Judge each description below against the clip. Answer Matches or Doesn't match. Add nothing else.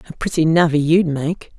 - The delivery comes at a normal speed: Matches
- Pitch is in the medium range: Matches